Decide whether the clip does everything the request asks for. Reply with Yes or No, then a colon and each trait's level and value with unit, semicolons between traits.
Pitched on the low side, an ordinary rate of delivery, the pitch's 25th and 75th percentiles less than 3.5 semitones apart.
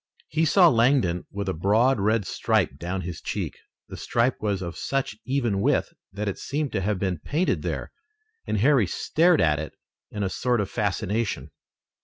No: low, 105 Hz; average, 180 wpm; wide, 5.6 semitones